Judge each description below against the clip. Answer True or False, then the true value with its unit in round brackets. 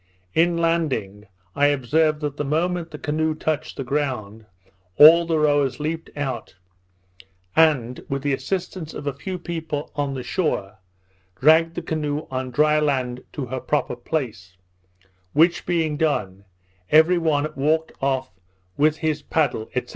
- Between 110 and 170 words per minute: True (145 wpm)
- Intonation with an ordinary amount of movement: True (3.4 semitones)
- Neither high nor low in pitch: True (150 Hz)